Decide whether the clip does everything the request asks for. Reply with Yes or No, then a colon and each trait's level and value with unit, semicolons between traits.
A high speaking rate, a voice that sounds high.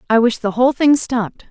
Yes: fast, 240 wpm; high, 240 Hz